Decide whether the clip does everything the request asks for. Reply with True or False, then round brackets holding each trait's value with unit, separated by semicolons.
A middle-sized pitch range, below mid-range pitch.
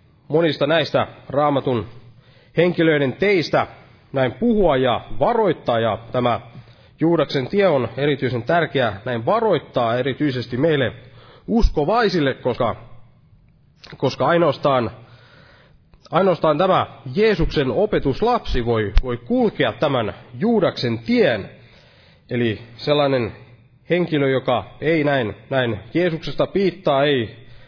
True (4.1 semitones; 130 Hz)